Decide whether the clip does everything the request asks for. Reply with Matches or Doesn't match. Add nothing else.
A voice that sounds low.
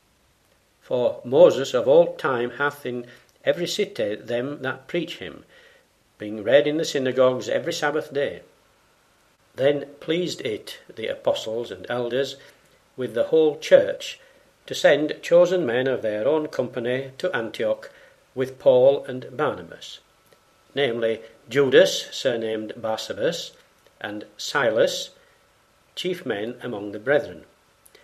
Doesn't match